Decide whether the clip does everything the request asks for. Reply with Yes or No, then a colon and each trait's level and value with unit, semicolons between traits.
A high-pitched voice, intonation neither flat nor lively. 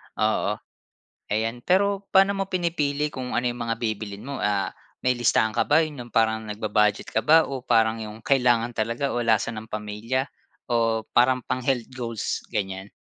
No: low, 120 Hz; average, 3.9 semitones